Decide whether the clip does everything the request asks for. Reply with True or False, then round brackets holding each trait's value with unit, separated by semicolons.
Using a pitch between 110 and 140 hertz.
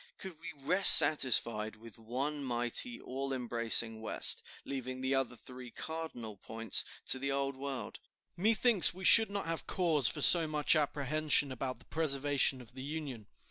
True (135 Hz)